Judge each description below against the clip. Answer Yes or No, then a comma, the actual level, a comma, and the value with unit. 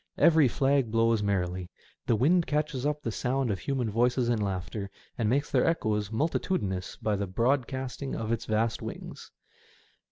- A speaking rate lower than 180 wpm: Yes, average, 165 wpm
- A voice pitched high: No, low, 115 Hz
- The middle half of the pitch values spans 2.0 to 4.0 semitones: No, average, 4.6 semitones